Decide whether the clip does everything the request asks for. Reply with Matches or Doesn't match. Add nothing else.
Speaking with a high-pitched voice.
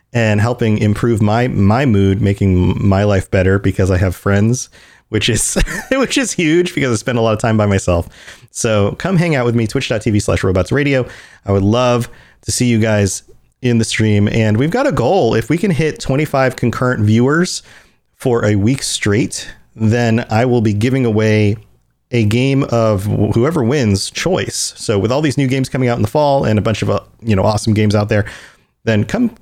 Doesn't match